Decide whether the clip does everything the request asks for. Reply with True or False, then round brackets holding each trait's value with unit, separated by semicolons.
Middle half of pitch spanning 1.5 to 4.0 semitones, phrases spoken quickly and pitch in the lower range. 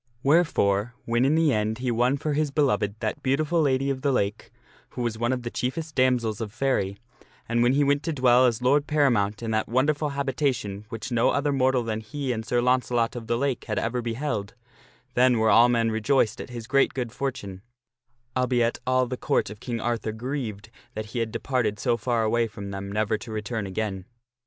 True (3.4 semitones; 210 wpm; 120 Hz)